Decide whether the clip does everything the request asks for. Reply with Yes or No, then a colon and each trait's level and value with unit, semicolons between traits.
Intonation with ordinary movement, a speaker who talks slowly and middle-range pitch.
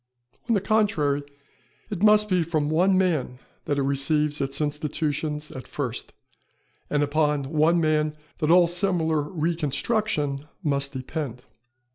Yes: average, 3.2 semitones; slow, 130 wpm; medium, 150 Hz